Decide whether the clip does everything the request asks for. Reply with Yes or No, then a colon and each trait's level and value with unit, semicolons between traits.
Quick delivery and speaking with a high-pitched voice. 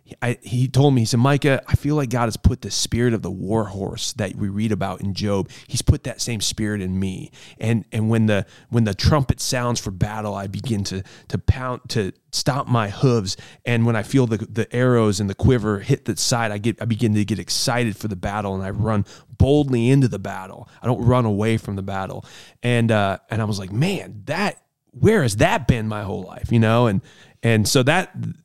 No: fast, 230 wpm; low, 115 Hz